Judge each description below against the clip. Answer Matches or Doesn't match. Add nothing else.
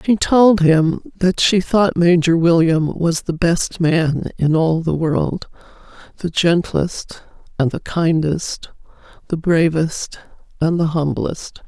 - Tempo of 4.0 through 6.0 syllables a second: Doesn't match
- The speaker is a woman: Matches